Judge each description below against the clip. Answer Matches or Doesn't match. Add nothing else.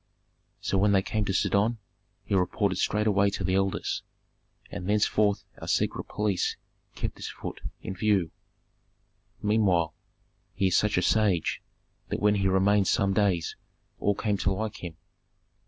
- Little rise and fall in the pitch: Matches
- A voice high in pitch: Doesn't match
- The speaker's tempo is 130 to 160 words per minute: Matches